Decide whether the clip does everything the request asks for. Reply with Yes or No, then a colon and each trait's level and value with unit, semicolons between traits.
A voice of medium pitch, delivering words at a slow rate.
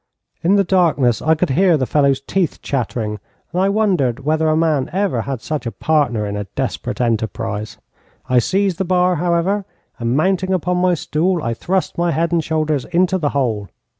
No: medium, 155 Hz; average, 190 wpm